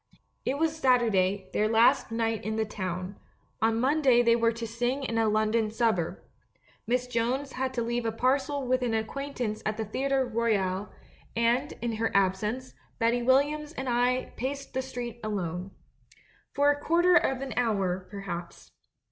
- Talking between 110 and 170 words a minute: Yes, average, 165 wpm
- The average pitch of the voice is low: No, high, 235 Hz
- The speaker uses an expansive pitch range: No, average, 3.4 semitones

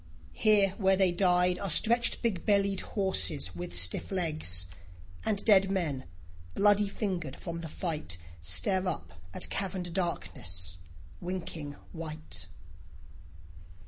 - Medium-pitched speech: Yes, medium, 175 Hz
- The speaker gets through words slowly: Yes, slow, 115 wpm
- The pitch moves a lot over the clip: Yes, wide, 6.4 semitones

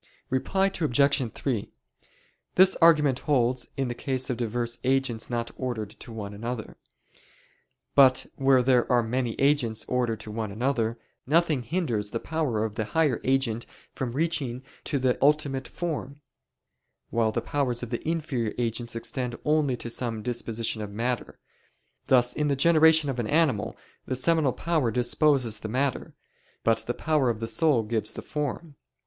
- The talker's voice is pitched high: No, low, 125 Hz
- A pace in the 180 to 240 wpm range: No, average, 160 wpm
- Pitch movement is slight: No, average, 3.8 semitones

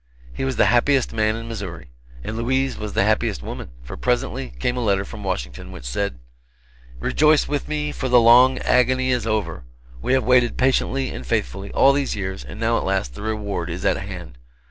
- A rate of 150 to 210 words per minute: Yes, average, 200 wpm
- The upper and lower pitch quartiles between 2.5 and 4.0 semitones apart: No, wide, 5.4 semitones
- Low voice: Yes, low, 110 Hz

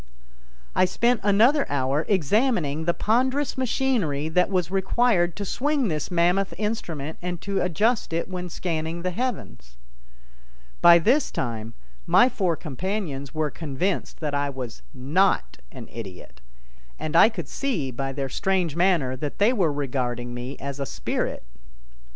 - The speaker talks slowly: No, average, 150 wpm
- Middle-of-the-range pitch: Yes, medium, 170 Hz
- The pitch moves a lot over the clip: Yes, wide, 6.4 semitones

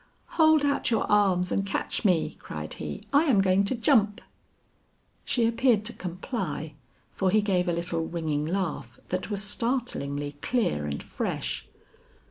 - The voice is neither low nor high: No, high, 195 Hz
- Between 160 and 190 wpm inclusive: No, average, 150 wpm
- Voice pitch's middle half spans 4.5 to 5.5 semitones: Yes, average, 5.2 semitones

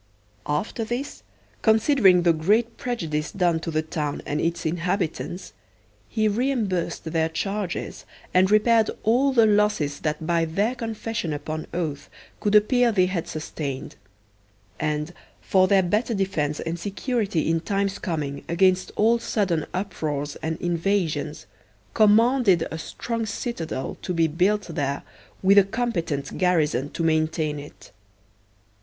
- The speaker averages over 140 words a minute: No, slow, 135 wpm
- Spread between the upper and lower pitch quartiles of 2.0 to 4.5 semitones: No, average, 5.0 semitones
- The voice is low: No, medium, 180 Hz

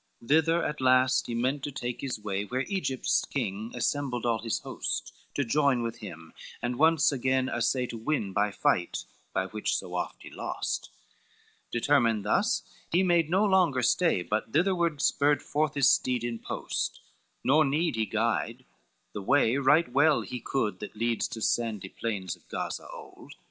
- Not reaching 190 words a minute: Yes, average, 175 wpm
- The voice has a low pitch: Yes, low, 125 Hz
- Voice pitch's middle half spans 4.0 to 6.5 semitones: Yes, average, 4.6 semitones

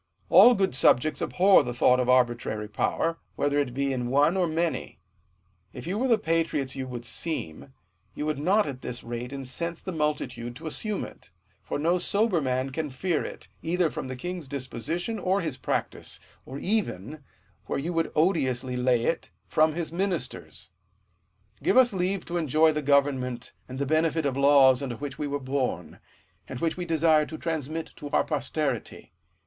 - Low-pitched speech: No, medium, 150 Hz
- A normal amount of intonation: Yes, average, 4.5 semitones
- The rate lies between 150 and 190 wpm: Yes, average, 180 wpm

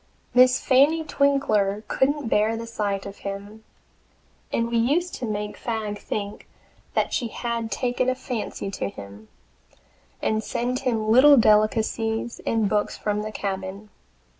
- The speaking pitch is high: Yes, high, 220 Hz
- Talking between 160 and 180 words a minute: No, average, 140 wpm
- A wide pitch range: No, average, 3.4 semitones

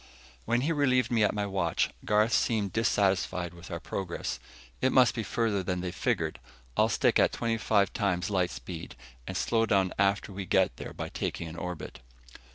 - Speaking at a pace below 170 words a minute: No, average, 185 wpm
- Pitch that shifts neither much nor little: Yes, average, 4.0 semitones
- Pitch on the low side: Yes, low, 100 Hz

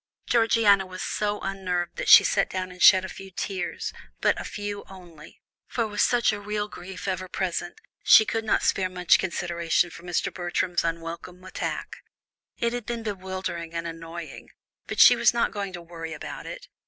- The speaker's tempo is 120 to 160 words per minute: No, average, 180 wpm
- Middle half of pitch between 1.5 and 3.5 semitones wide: Yes, average, 2.9 semitones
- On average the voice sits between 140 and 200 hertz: Yes, medium, 185 Hz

